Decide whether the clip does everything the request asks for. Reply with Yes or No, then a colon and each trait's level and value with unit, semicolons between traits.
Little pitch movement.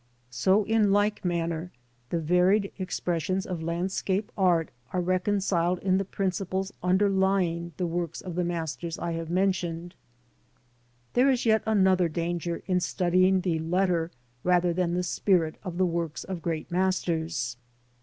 Yes: narrow, 2.1 semitones